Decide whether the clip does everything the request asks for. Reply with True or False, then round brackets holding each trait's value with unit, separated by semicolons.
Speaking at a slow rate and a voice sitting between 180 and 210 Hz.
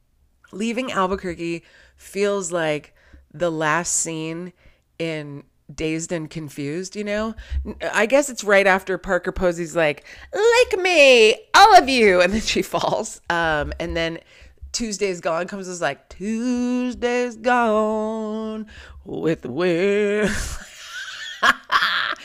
True (115 wpm; 185 Hz)